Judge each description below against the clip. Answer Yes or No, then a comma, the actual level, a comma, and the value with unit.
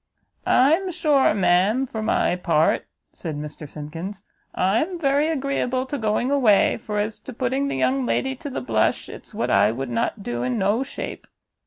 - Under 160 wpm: No, average, 175 wpm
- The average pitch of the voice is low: No, high, 215 Hz